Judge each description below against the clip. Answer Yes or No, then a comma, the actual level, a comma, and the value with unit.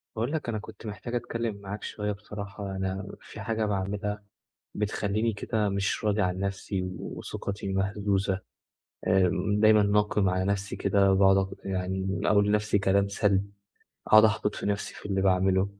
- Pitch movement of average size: No, narrow, 1.5 semitones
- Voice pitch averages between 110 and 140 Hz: No, low, 100 Hz